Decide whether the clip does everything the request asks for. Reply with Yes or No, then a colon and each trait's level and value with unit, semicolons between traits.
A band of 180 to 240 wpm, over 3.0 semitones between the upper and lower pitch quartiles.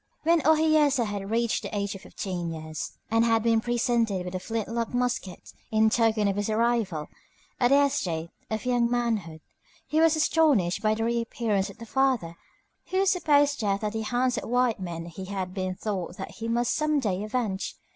Yes: average, 190 wpm; average, 4.1 semitones